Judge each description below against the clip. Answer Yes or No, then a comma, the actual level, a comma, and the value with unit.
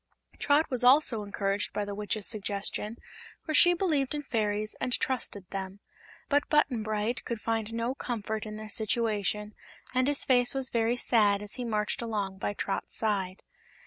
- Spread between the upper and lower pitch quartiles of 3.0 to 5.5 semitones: Yes, average, 3.4 semitones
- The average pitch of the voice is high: Yes, high, 220 Hz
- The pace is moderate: Yes, average, 170 wpm